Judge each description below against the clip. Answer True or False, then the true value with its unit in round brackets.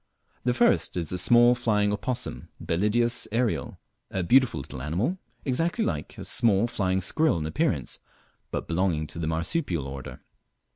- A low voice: True (95 Hz)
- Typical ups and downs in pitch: False (6.6 semitones)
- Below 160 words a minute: True (150 wpm)